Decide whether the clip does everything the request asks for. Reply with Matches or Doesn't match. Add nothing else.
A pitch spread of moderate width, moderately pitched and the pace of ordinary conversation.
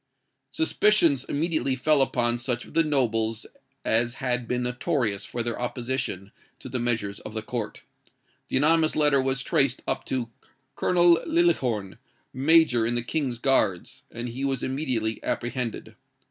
Doesn't match